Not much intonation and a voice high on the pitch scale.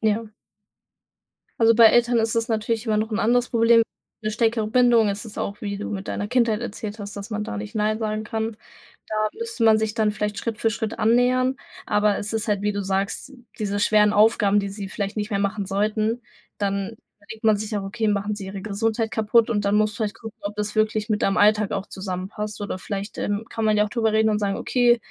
Yes: narrow, 1.7 semitones; high, 215 Hz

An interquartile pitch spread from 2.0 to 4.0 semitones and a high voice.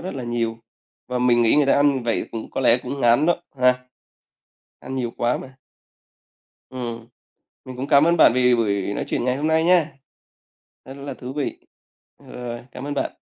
No: average, 2.9 semitones; low, 125 Hz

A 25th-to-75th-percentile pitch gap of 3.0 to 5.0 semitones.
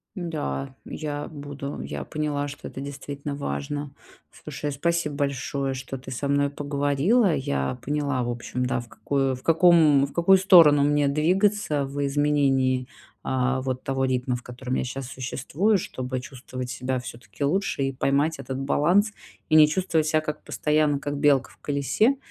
No: narrow, 2.6 semitones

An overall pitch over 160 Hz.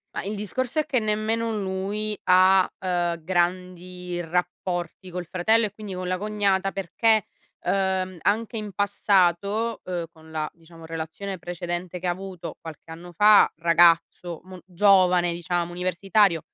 Yes: medium, 185 Hz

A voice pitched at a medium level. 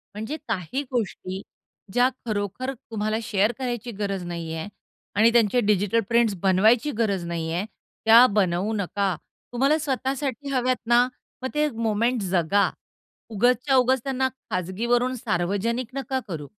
No: high, 225 Hz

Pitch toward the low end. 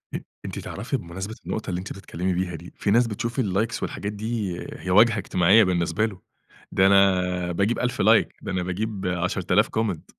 Yes: very low, 95 Hz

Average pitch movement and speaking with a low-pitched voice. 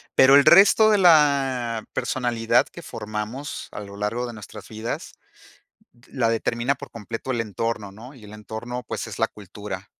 Yes: average, 3.7 semitones; low, 115 Hz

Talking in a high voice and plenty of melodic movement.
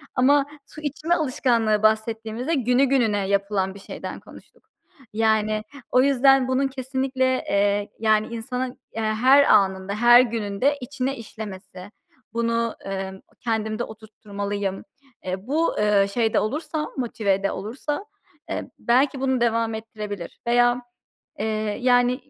No: high, 230 Hz; average, 3.7 semitones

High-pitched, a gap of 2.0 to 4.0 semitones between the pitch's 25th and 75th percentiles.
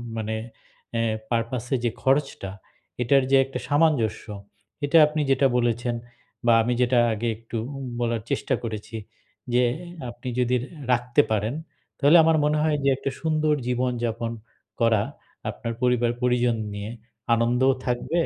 No: low, 120 Hz; average, 2.7 semitones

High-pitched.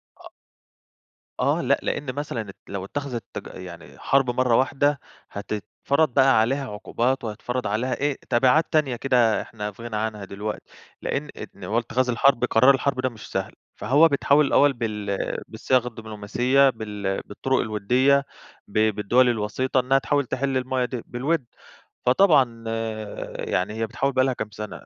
No: low, 125 Hz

